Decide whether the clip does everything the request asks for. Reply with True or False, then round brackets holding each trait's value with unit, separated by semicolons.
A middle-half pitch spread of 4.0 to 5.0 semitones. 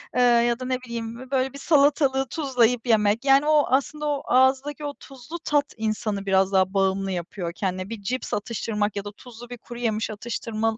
True (4.3 semitones)